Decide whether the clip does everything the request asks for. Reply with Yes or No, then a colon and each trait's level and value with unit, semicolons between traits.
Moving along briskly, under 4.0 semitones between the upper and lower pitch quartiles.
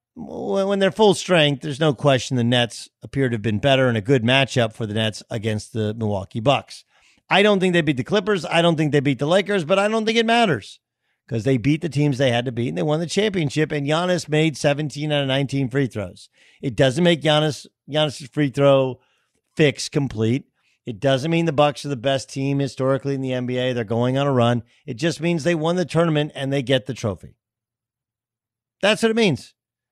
No: fast, 225 wpm; average, 4.6 semitones